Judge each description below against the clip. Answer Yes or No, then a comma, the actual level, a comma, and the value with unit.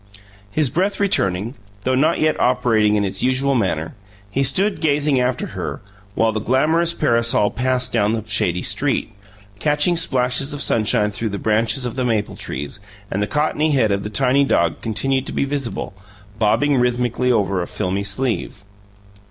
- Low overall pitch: Yes, low, 125 Hz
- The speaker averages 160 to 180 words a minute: Yes, average, 170 wpm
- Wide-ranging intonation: No, average, 4.8 semitones